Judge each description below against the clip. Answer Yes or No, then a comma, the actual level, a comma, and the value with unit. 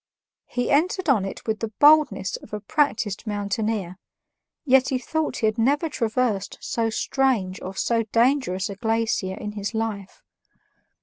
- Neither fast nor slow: Yes, average, 150 wpm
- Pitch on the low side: No, high, 225 Hz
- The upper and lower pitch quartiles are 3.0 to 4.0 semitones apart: No, average, 4.6 semitones